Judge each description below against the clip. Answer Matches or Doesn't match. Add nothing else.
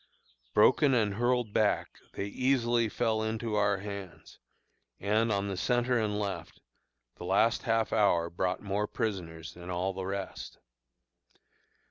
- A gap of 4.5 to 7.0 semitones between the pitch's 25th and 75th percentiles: Doesn't match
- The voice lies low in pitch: Matches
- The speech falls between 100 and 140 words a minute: Matches